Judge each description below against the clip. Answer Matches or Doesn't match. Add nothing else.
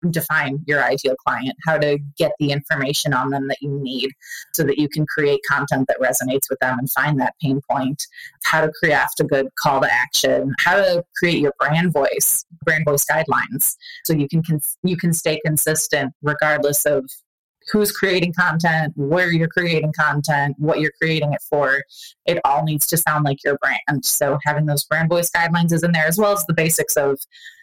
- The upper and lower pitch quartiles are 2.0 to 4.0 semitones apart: Matches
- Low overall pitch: Doesn't match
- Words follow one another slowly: Doesn't match